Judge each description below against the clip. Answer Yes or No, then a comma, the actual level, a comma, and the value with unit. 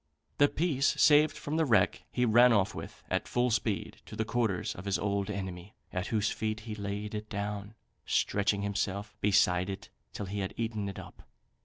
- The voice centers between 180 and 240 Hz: No, low, 105 Hz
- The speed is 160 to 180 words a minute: No, average, 190 wpm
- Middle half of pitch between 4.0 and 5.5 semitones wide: No, narrow, 2.4 semitones